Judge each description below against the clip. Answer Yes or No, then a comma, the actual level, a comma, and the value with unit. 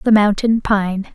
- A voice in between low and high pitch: No, high, 205 Hz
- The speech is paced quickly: No, average, 155 wpm